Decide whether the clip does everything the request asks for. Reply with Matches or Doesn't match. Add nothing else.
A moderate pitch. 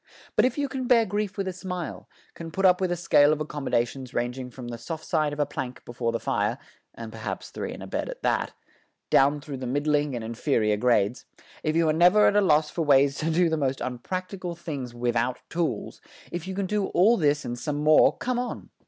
Matches